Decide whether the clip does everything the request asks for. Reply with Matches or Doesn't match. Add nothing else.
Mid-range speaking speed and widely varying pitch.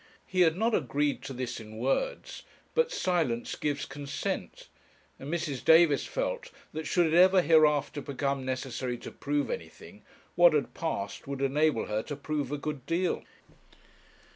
Doesn't match